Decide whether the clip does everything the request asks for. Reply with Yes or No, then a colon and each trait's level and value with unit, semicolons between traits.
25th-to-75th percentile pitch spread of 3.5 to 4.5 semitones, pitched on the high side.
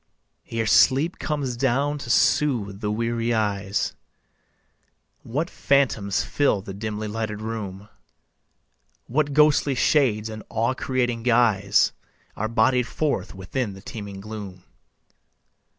No: average, 4.0 semitones; low, 115 Hz